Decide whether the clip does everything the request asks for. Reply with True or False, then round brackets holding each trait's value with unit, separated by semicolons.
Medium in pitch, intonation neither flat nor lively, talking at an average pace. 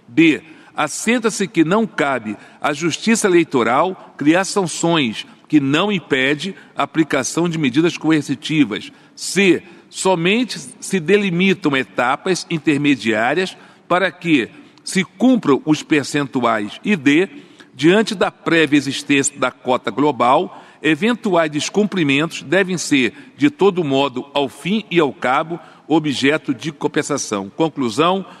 False (160 Hz; 5.0 semitones; 115 wpm)